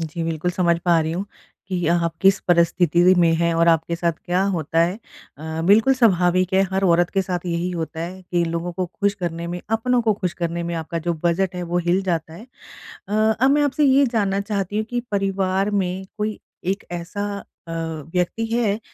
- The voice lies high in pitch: No, medium, 180 Hz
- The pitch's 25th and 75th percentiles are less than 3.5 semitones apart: Yes, average, 2.9 semitones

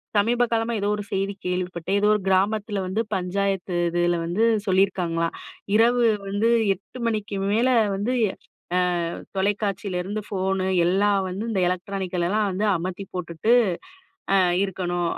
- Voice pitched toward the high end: Yes, high, 195 Hz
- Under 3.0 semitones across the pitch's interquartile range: Yes, narrow, 2.5 semitones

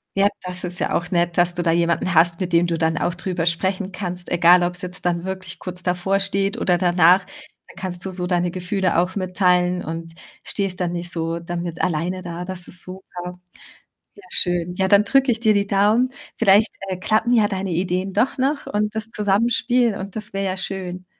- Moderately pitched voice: Yes, medium, 180 Hz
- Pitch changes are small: Yes, narrow, 2.0 semitones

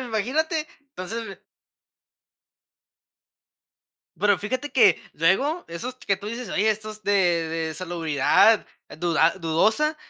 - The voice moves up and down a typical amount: No, wide, 6.7 semitones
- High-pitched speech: Yes, high, 205 Hz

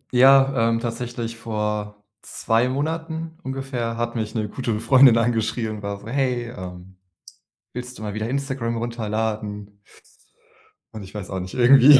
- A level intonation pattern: No, average, 3.2 semitones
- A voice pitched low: Yes, low, 115 Hz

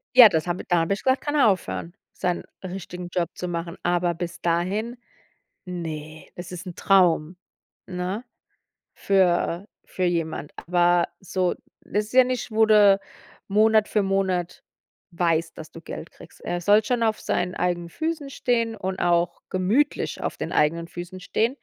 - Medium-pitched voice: Yes, medium, 180 Hz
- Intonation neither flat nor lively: Yes, average, 3.5 semitones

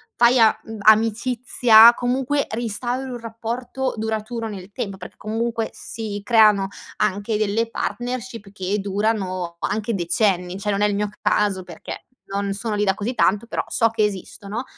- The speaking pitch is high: Yes, high, 215 Hz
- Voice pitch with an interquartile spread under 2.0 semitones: No, narrow, 2.6 semitones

